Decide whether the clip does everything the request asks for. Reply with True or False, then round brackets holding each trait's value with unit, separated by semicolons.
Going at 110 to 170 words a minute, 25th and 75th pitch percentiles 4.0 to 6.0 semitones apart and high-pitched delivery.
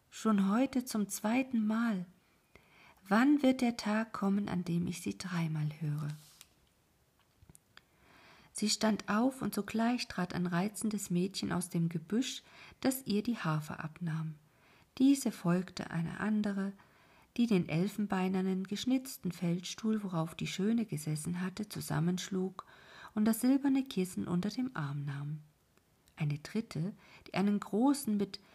True (130 wpm; 4.4 semitones; 195 Hz)